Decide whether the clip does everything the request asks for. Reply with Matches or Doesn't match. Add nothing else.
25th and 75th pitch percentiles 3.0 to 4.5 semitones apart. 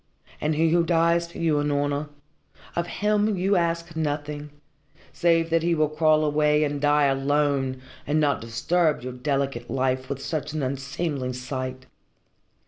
Matches